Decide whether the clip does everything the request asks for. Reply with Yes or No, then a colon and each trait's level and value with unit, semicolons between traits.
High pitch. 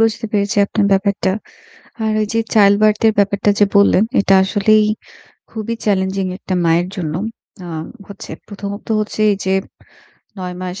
Yes: high, 200 Hz